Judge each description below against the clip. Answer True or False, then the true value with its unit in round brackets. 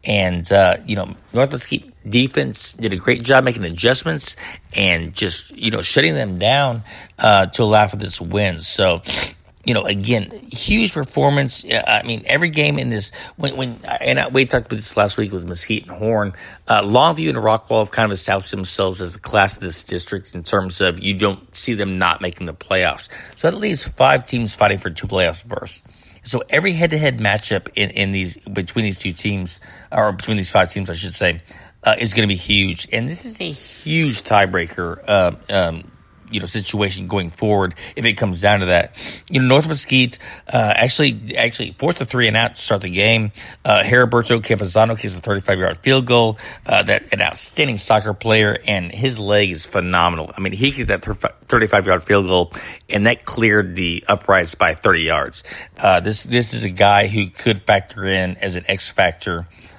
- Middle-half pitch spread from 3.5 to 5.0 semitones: True (4.1 semitones)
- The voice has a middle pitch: False (105 Hz)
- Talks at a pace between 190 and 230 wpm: True (200 wpm)